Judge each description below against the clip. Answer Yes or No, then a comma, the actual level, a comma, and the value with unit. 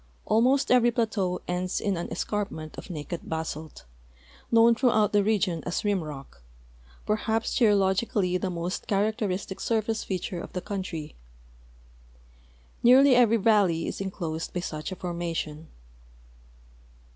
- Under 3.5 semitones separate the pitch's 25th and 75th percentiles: No, average, 4.2 semitones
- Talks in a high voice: Yes, high, 195 Hz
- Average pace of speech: No, slow, 125 wpm